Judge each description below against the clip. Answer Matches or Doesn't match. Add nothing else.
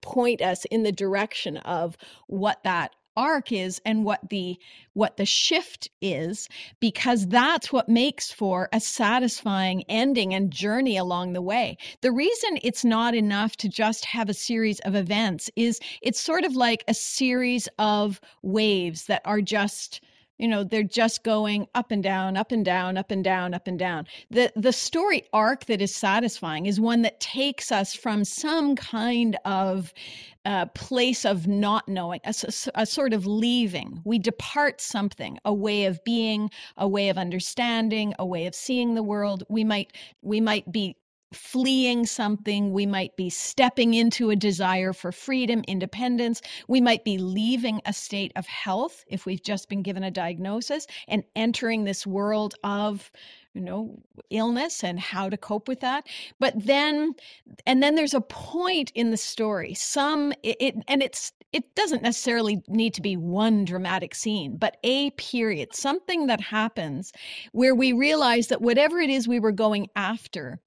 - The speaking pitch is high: Matches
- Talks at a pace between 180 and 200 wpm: Doesn't match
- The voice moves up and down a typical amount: Matches